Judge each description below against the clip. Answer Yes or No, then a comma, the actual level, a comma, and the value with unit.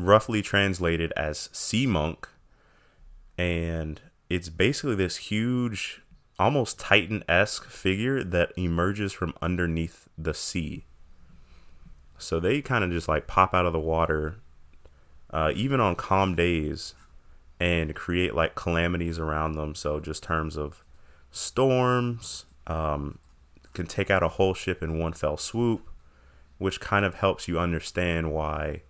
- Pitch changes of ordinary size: Yes, average, 3.9 semitones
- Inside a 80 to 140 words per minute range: Yes, slow, 135 wpm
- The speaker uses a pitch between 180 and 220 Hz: No, very low, 85 Hz